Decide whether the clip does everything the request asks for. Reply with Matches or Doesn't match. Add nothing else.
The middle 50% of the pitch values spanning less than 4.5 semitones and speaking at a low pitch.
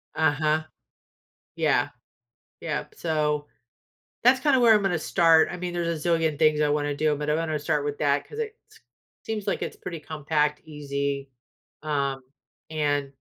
Doesn't match